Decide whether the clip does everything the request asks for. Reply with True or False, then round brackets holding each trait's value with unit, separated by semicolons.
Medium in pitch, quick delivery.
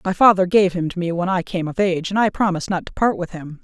True (180 Hz; 315 wpm)